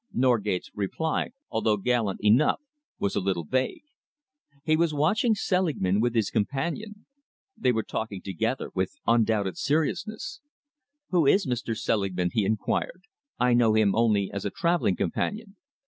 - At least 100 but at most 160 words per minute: Yes, average, 140 wpm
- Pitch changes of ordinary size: No, wide, 7.8 semitones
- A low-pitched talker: Yes, low, 115 Hz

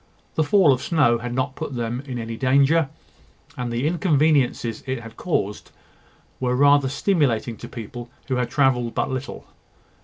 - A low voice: Yes, low, 130 Hz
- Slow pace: No, average, 160 wpm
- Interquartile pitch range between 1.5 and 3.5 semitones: Yes, average, 3.2 semitones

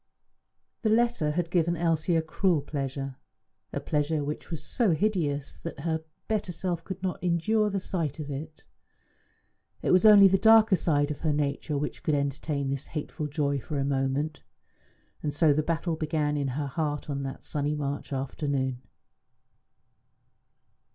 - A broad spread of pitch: No, average, 3.4 semitones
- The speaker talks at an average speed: Yes, average, 160 wpm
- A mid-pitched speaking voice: Yes, medium, 150 Hz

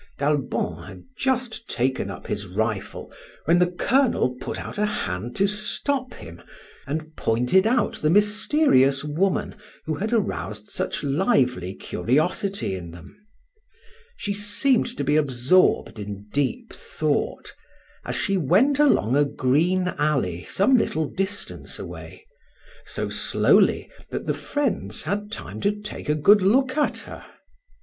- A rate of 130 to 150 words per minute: Yes, average, 140 wpm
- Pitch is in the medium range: Yes, medium, 175 Hz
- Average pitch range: No, wide, 8.5 semitones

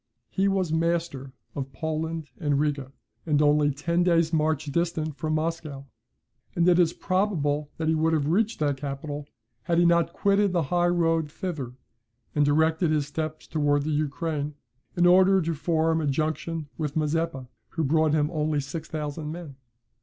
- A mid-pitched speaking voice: Yes, medium, 155 Hz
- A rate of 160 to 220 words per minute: Yes, average, 165 wpm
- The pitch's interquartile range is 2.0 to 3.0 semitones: Yes, narrow, 2.4 semitones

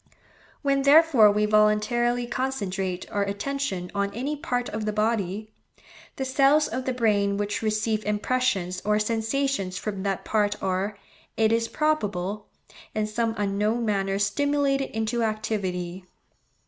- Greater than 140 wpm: No, slow, 135 wpm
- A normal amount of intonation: Yes, average, 3.5 semitones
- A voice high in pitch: Yes, high, 215 Hz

